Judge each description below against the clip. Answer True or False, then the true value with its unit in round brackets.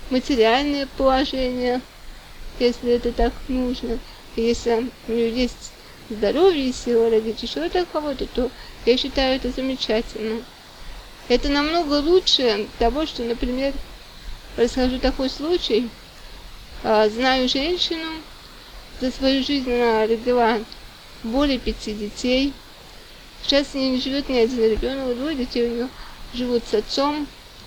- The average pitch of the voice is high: True (250 Hz)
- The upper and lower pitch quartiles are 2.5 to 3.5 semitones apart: True (2.8 semitones)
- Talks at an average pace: True (125 wpm)